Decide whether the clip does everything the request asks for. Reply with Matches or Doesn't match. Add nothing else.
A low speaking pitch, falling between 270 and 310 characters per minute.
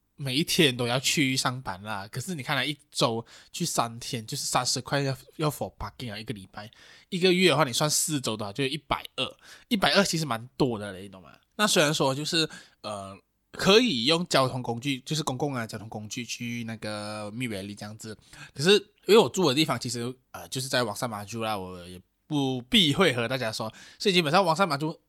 Doesn't match